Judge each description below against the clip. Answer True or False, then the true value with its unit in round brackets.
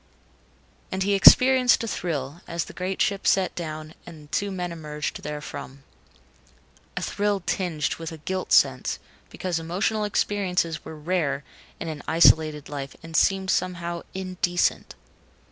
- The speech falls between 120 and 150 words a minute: True (140 wpm)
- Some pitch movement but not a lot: True (3.5 semitones)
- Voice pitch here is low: False (170 Hz)